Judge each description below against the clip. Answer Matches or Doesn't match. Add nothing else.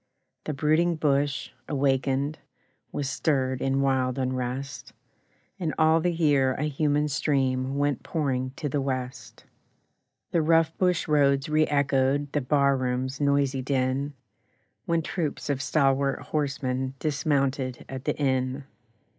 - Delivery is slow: Matches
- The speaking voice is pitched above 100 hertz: Matches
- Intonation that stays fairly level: Matches